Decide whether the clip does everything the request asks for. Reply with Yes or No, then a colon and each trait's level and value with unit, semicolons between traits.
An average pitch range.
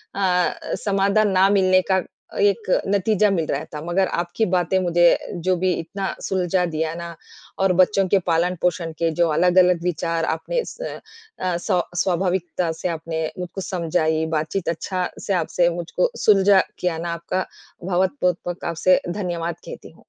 No: narrow, 2.1 semitones